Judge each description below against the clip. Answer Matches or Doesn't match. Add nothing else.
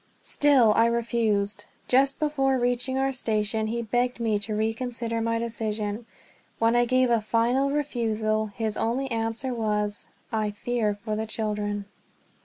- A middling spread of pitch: Doesn't match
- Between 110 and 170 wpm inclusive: Matches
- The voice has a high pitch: Matches